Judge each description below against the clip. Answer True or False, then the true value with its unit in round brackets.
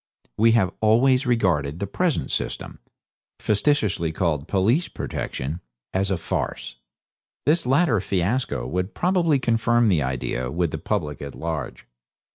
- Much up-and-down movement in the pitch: True (7.3 semitones)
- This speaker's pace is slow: True (130 wpm)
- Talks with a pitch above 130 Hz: False (100 Hz)